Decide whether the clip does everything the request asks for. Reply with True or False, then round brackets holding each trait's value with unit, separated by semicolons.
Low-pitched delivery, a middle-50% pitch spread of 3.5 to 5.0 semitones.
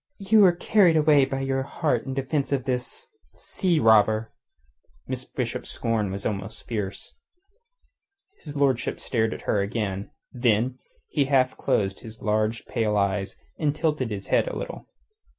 True (125 Hz; 4.6 semitones)